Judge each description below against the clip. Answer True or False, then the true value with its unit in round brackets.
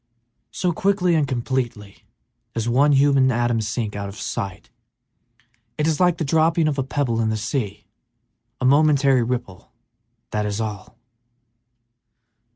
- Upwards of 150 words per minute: False (140 wpm)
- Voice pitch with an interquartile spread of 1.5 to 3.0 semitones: False (5.1 semitones)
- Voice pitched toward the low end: True (130 Hz)